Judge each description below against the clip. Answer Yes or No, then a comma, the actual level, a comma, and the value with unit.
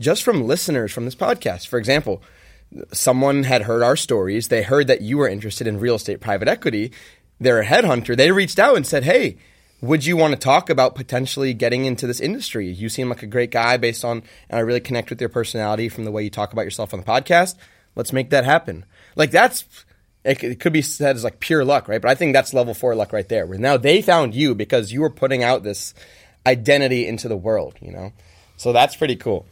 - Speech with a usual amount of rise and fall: Yes, average, 3.2 semitones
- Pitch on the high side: No, low, 120 Hz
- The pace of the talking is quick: Yes, fast, 230 wpm